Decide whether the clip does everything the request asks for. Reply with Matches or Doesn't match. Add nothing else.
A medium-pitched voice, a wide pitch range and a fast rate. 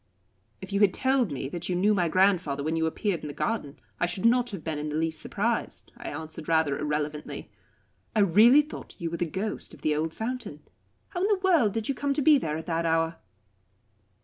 Matches